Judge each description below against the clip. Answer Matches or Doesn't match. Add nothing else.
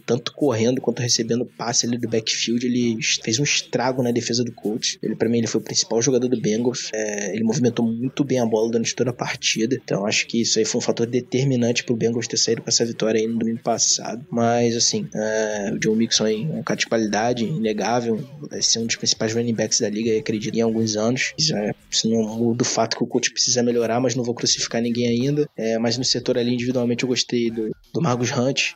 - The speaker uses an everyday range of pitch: Doesn't match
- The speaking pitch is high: Doesn't match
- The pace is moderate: Doesn't match